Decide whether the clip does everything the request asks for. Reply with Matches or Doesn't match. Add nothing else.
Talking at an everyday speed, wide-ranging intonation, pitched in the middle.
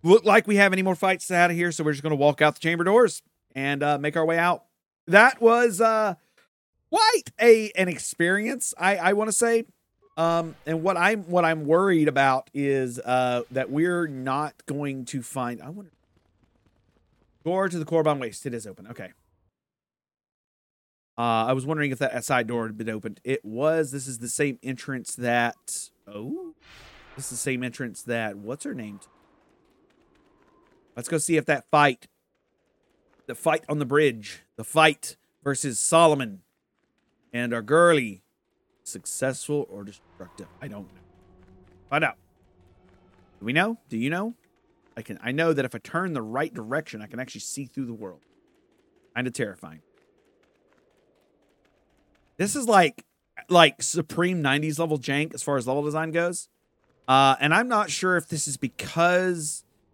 Matches